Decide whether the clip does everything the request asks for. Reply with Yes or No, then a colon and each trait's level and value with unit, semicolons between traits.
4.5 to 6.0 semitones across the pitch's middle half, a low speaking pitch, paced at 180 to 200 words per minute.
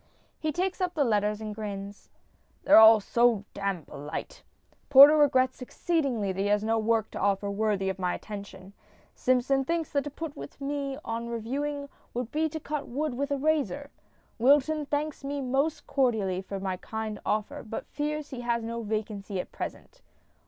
No: wide, 5.6 semitones; high, 240 Hz; average, 185 wpm